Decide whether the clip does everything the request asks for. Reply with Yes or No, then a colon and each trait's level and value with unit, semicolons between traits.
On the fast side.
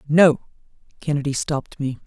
No: slow, 115 wpm